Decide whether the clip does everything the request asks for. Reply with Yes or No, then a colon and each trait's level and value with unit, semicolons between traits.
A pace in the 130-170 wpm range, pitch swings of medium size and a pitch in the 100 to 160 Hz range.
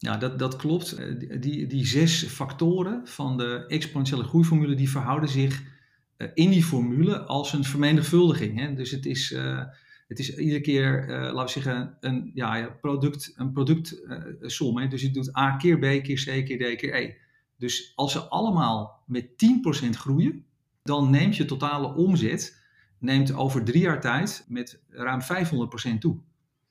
Yes: average, 155 wpm; average, 3.2 semitones; low, 135 Hz